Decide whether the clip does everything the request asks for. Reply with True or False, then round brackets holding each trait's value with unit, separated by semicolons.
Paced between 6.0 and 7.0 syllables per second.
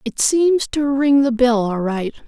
False (4.0 syllables/s)